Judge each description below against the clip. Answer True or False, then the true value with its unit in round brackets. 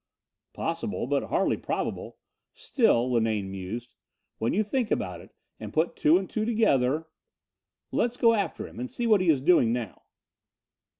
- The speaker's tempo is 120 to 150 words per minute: False (160 wpm)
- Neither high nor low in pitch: True (155 Hz)